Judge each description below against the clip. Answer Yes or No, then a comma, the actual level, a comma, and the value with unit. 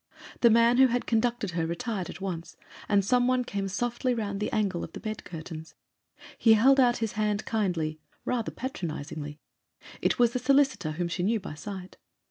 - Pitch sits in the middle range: No, high, 210 Hz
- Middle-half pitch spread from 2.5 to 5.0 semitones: No, wide, 5.5 semitones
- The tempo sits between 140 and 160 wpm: No, average, 180 wpm